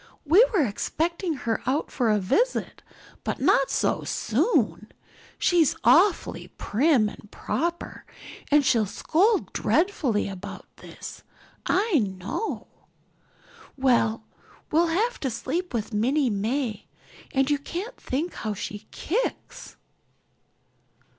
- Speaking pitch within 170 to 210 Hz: No, very high, 275 Hz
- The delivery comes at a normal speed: No, slow, 115 wpm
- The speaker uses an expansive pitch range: Yes, wide, 7.9 semitones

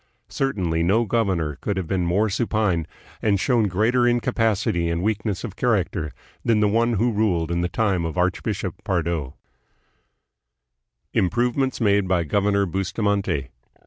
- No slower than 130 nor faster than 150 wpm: Yes, average, 140 wpm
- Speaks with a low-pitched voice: Yes, low, 100 Hz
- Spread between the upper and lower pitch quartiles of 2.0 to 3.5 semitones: No, average, 4.2 semitones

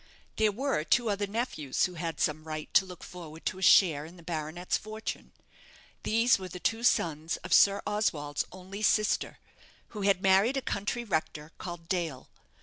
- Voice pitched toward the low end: No, medium, 185 Hz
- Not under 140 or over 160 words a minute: No, average, 175 wpm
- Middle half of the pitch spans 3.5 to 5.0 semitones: Yes, average, 4.7 semitones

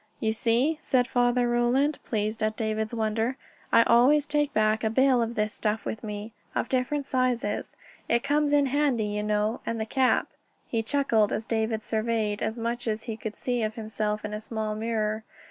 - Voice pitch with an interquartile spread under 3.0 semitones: Yes, narrow, 2.5 semitones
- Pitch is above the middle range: Yes, high, 225 Hz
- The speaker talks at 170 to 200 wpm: Yes, average, 190 wpm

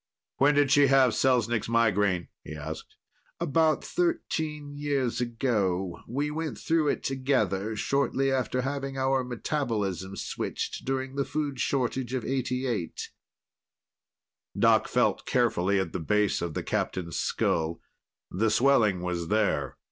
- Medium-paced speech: No, slow, 130 wpm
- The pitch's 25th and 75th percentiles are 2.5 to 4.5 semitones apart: No, wide, 5.5 semitones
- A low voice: Yes, low, 125 Hz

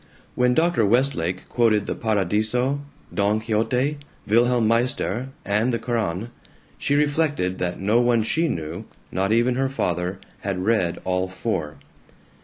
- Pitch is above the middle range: No, low, 110 Hz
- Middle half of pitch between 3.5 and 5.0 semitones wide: Yes, average, 4.7 semitones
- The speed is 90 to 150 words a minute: Yes, slow, 135 wpm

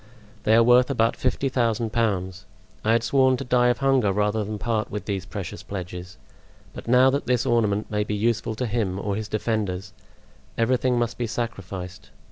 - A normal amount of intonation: Yes, average, 3.3 semitones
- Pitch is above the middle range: No, low, 110 Hz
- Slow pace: No, average, 185 wpm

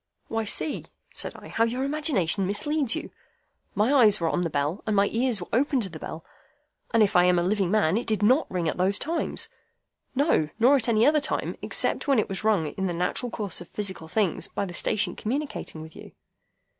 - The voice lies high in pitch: Yes, high, 210 Hz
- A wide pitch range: Yes, wide, 5.7 semitones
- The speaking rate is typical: No, fast, 220 wpm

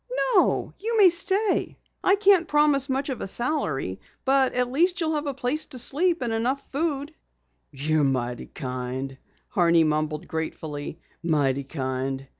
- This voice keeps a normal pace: Yes, average, 150 wpm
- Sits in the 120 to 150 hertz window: No, high, 245 Hz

